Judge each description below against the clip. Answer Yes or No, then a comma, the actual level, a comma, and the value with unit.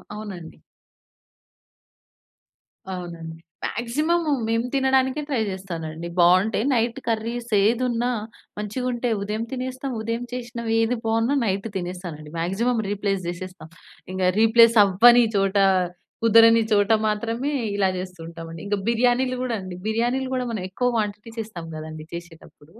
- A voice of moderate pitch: No, high, 220 Hz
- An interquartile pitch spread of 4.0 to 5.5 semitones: Yes, average, 4.5 semitones